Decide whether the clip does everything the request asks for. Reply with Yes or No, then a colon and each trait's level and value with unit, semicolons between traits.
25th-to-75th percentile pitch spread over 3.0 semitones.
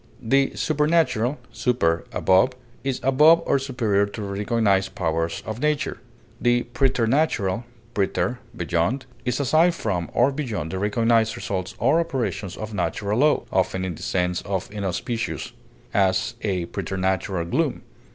Yes: wide, 5.5 semitones